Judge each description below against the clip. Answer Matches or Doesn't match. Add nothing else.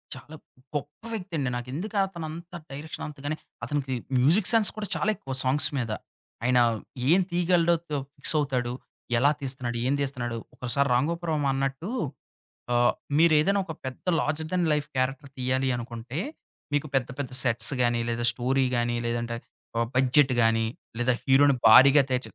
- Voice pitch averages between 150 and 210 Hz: Doesn't match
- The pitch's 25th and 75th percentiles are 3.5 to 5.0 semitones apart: Matches